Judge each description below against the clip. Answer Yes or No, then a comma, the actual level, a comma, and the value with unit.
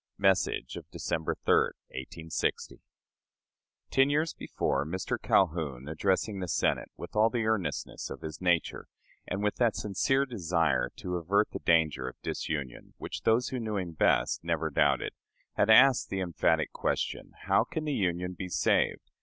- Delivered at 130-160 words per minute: Yes, average, 155 wpm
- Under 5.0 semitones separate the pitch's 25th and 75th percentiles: No, average, 5.3 semitones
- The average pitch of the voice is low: Yes, very low, 90 Hz